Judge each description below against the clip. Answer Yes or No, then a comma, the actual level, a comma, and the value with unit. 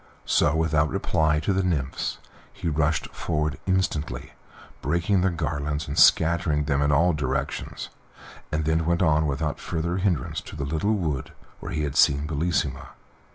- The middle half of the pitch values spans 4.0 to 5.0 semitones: No, narrow, 2.6 semitones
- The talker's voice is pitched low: Yes, very low, 80 Hz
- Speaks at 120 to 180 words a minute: Yes, average, 155 wpm